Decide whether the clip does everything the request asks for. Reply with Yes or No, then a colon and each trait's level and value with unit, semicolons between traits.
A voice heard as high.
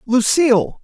Yes: very high, 250 Hz